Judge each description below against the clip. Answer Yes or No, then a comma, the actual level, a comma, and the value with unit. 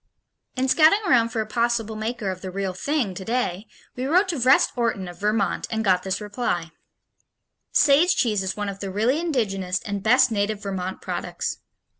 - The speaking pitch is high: Yes, high, 215 Hz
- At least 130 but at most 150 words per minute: No, average, 180 wpm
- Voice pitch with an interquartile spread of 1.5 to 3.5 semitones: No, average, 4.5 semitones